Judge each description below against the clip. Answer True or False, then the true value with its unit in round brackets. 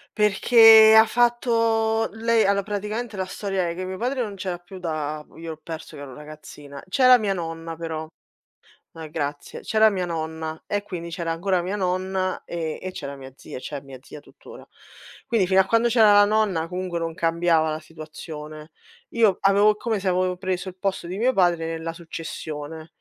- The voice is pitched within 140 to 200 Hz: True (185 Hz)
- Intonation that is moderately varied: True (4.4 semitones)